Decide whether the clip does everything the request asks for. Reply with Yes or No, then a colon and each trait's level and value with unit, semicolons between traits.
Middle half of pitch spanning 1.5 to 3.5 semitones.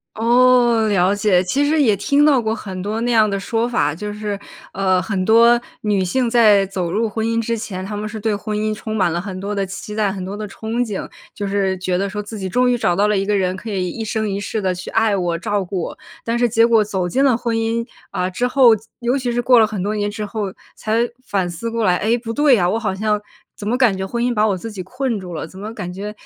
Yes: average, 3.1 semitones